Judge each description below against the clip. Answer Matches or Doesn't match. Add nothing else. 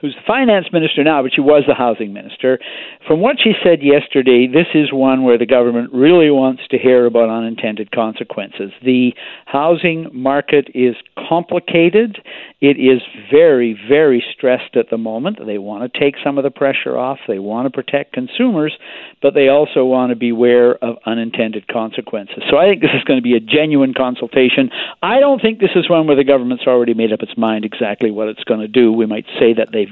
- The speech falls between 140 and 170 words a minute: Doesn't match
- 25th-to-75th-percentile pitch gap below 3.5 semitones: Doesn't match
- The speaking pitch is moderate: Doesn't match